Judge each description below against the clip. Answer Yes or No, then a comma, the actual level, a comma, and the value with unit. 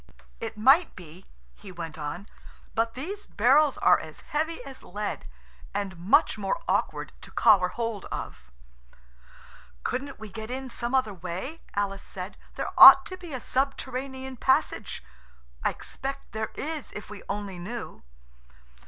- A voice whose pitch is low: No, high, 225 Hz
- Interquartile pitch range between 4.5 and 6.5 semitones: Yes, wide, 5.5 semitones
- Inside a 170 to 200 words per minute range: No, average, 145 wpm